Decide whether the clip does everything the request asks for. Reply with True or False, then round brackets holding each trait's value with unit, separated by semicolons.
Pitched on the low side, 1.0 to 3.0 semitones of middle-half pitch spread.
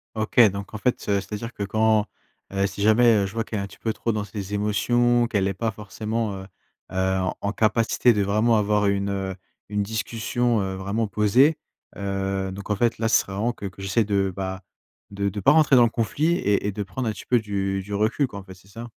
True (105 Hz; 2.5 semitones)